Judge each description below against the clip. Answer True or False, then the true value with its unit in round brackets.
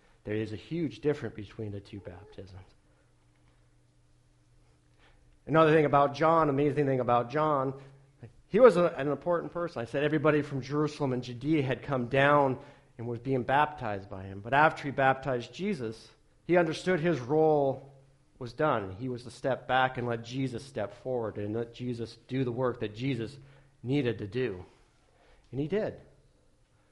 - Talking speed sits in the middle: True (165 wpm)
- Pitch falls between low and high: False (130 Hz)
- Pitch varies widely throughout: False (4.5 semitones)